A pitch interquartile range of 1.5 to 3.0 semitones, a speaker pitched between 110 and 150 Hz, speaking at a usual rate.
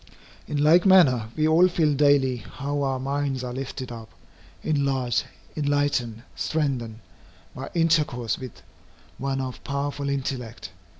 No: narrow, 2.5 semitones; medium, 140 Hz; slow, 125 wpm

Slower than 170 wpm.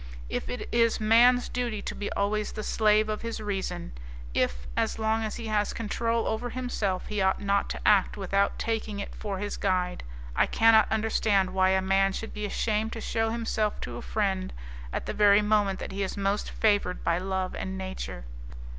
No: average, 195 wpm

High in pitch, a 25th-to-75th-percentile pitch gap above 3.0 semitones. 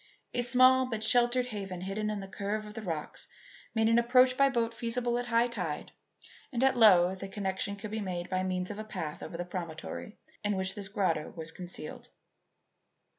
Yes: high, 210 Hz; average, 4.2 semitones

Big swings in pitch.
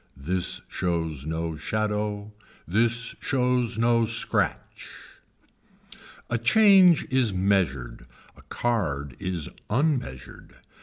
Yes: wide, 6.6 semitones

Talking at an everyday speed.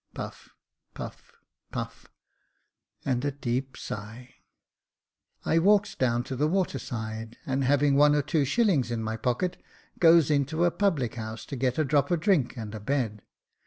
Yes: average, 160 wpm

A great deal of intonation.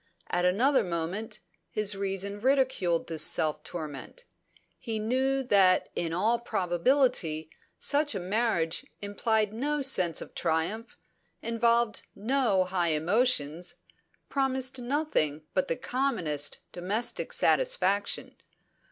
Yes: wide, 6.4 semitones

